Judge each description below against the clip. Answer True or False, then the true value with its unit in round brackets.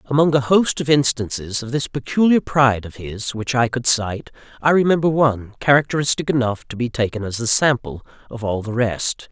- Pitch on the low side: True (125 Hz)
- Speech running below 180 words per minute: False (195 wpm)